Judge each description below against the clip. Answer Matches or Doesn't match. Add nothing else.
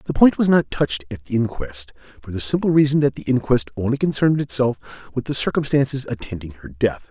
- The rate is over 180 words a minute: Matches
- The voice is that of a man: Matches